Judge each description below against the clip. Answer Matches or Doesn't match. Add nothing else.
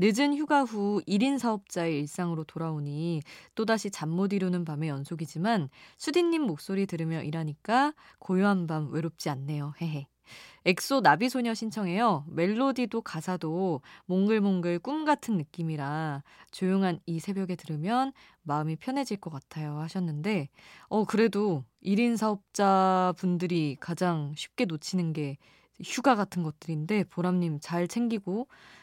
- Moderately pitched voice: Matches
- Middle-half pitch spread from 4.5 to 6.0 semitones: Matches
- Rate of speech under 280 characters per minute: Doesn't match